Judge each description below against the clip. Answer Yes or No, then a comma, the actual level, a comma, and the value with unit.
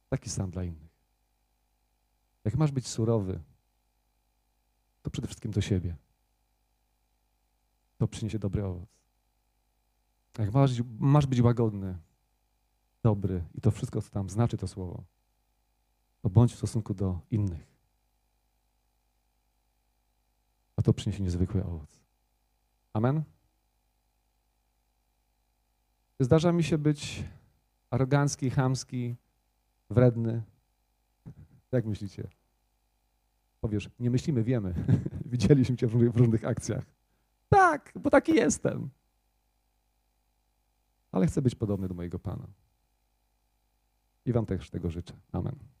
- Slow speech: Yes, slow, 105 wpm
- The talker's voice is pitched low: Yes, very low, 75 Hz